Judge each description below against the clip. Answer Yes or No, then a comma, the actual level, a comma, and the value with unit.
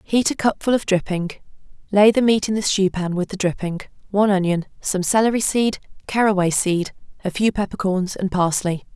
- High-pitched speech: Yes, high, 195 Hz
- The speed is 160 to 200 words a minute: Yes, average, 180 wpm